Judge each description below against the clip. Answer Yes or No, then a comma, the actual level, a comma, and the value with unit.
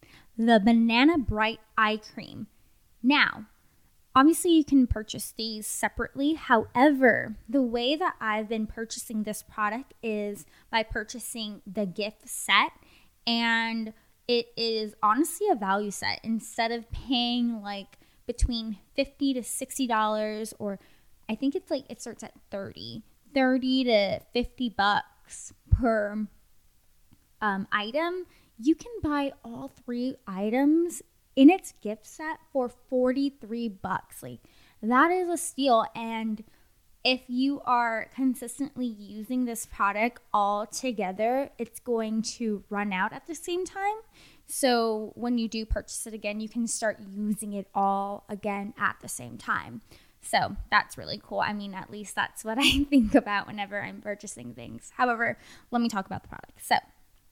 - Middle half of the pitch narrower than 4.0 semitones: Yes, average, 3.6 semitones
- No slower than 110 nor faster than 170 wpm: Yes, average, 145 wpm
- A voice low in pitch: No, high, 230 Hz